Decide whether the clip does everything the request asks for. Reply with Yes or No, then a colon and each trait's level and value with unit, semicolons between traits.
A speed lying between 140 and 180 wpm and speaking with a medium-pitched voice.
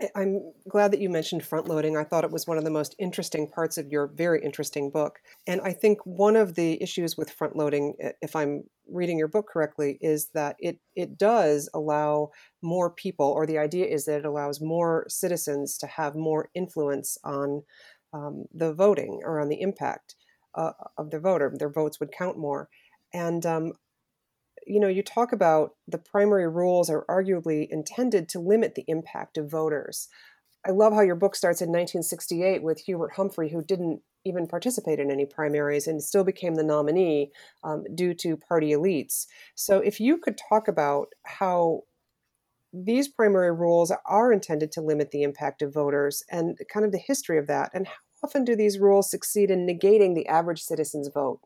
No: average, 190 wpm; medium, 165 Hz